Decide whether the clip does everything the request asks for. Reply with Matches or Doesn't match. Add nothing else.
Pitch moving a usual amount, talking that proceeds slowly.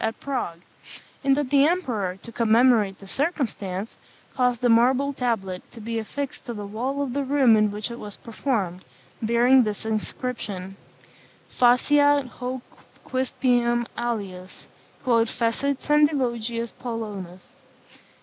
Matches